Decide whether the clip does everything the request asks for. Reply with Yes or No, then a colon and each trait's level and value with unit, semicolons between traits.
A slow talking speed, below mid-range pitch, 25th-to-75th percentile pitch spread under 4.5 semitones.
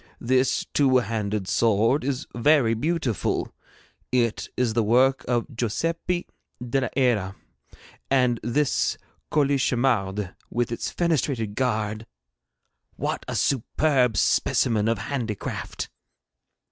Yes: slow, 105 wpm; low, 120 Hz; average, 3.6 semitones